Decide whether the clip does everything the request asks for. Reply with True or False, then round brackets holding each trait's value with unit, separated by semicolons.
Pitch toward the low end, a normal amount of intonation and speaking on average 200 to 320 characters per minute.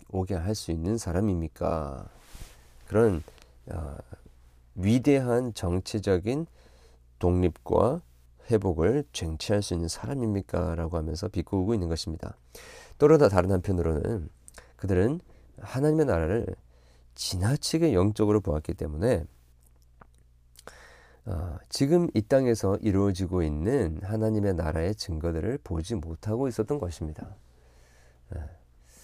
False (90 Hz; 6.2 semitones; 255 characters per minute)